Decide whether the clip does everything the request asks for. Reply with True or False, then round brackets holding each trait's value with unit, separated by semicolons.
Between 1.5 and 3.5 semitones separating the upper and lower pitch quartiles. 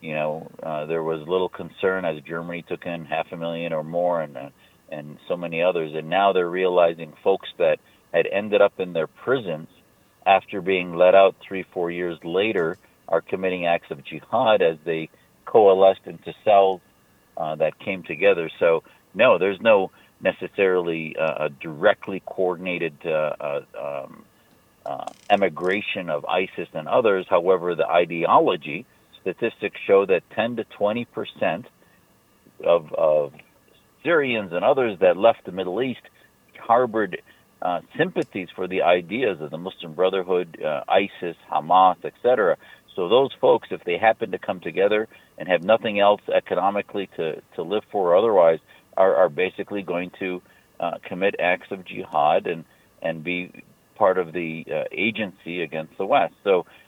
True (2.7 semitones)